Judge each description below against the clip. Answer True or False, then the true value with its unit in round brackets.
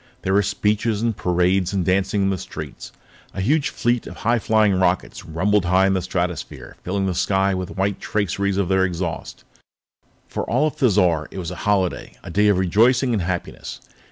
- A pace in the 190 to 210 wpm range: True (195 wpm)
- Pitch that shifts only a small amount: True (2.3 semitones)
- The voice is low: True (95 Hz)